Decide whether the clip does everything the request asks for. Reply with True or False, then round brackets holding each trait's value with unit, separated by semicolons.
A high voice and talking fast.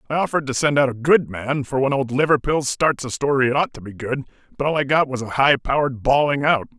False (135 Hz; 265 wpm)